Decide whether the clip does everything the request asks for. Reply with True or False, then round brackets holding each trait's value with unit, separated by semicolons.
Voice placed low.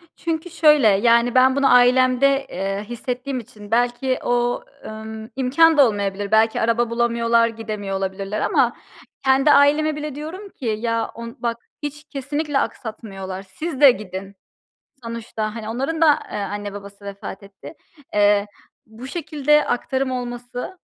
False (240 Hz)